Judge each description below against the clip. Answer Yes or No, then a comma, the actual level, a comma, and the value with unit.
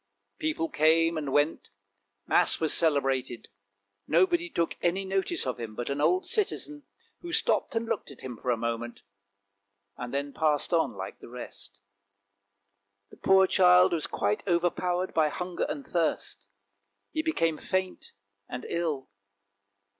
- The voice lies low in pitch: No, medium, 165 Hz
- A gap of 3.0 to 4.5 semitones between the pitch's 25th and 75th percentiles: No, average, 5.2 semitones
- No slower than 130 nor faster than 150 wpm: Yes, average, 145 wpm